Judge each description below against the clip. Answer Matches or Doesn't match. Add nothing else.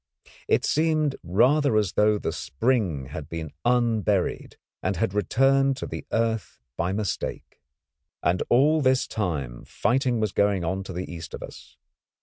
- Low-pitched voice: Matches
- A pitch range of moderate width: Doesn't match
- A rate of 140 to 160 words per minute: Matches